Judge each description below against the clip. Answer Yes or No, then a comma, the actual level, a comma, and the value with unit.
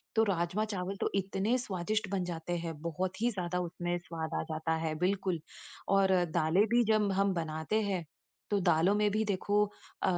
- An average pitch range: Yes, average, 3.1 semitones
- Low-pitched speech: No, medium, 185 Hz